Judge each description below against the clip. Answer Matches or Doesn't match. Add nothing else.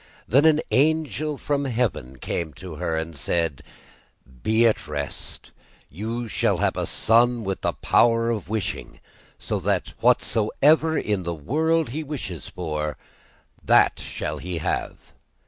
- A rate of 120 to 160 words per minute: Matches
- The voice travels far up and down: Matches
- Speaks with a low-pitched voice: Matches